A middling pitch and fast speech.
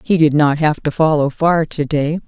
Yes: medium, 155 Hz; fast, 235 wpm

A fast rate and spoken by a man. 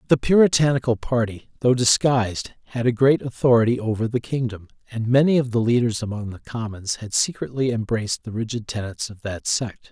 No: average, 175 wpm; male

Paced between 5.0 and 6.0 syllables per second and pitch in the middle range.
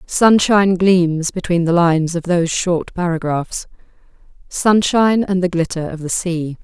No: 4.6 syllables/s; medium, 175 Hz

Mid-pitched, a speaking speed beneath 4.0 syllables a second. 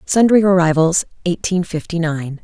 No: medium, 175 Hz; 4.7 syllables/s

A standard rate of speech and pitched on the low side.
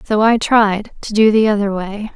No: average, 195 wpm; high, 210 Hz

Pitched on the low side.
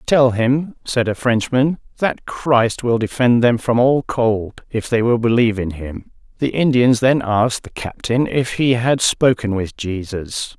Yes: low, 120 Hz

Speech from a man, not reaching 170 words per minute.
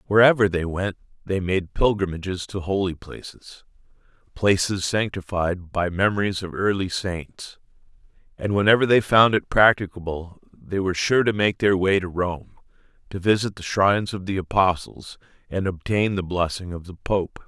Yes: male; average, 150 wpm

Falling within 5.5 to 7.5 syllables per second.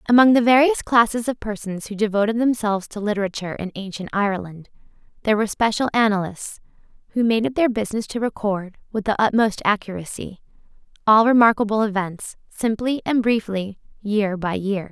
Yes: 5.8 syllables/s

